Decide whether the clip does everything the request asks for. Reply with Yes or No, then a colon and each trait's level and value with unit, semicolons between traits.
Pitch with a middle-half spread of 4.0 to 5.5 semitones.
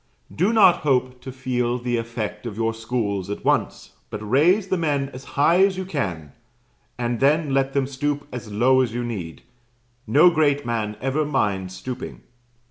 Yes: average, 4.4 semitones